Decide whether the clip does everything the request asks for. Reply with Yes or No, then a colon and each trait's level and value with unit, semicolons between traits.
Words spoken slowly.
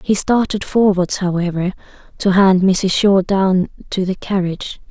No: average, 145 wpm